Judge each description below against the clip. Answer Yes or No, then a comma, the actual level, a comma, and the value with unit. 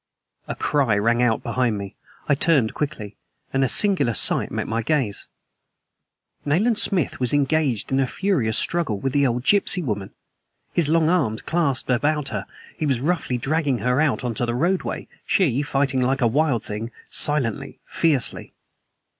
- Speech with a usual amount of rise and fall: Yes, average, 4.8 semitones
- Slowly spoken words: No, average, 165 wpm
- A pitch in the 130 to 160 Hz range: Yes, low, 135 Hz